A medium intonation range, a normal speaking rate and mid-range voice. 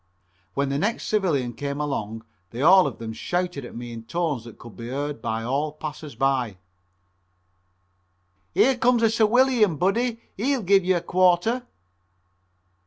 No: wide, 8.5 semitones; average, 155 wpm; medium, 155 Hz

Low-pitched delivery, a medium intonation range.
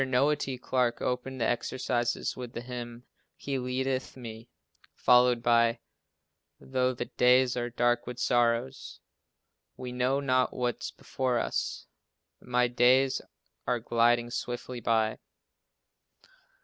No: low, 125 Hz; narrow, 1.2 semitones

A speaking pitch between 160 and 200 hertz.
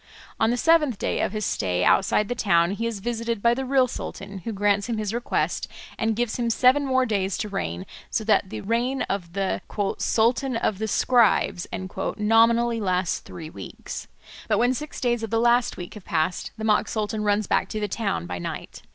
No: high, 220 Hz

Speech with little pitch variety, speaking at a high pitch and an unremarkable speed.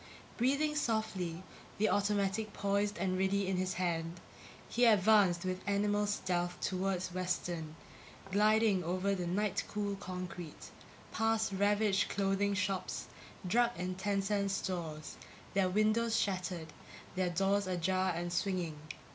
No: narrow, 2.2 semitones; high, 195 Hz; slow, 125 wpm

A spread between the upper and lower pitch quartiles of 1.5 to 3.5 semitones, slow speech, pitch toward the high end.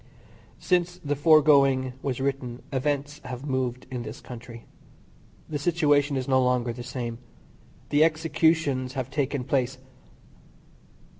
No: narrow, 2.6 semitones; slow, 125 wpm; low, 135 Hz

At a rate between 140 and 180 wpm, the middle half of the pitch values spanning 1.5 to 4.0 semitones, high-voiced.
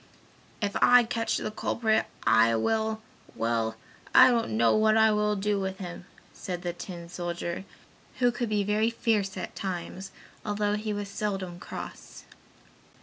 Yes: average, 150 wpm; average, 3.7 semitones; high, 205 Hz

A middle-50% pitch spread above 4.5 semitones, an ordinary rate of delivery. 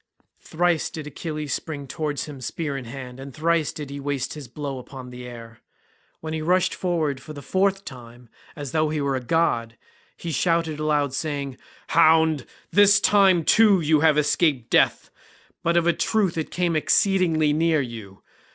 No: average, 3.5 semitones; average, 170 wpm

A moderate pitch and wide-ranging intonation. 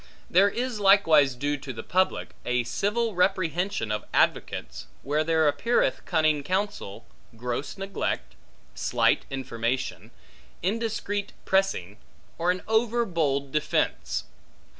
Yes: medium, 165 Hz; wide, 6.8 semitones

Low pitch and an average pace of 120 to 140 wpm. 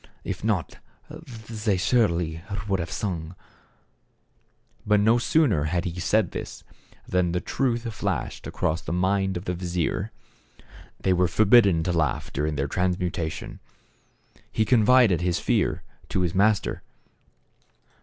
Yes: very low, 90 Hz; slow, 135 wpm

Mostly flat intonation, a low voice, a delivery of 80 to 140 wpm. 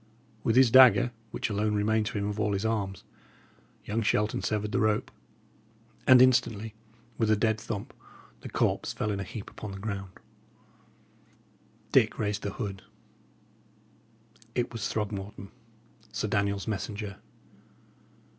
Yes: narrow, 1.7 semitones; low, 105 Hz; slow, 135 wpm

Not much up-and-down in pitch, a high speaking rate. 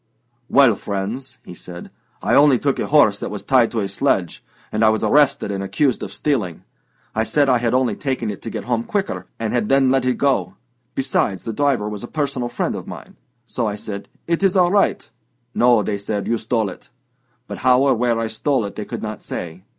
No: average, 4.5 semitones; fast, 220 wpm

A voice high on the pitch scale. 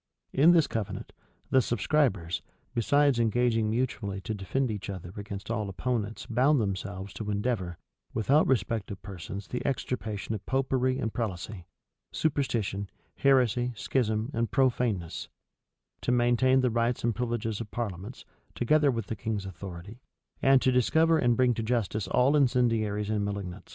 No: low, 115 Hz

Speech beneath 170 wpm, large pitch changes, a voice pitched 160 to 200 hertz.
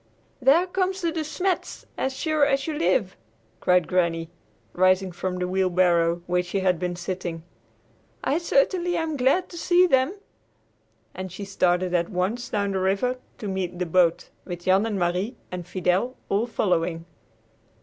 Yes: average, 160 wpm; wide, 7.1 semitones; high, 190 Hz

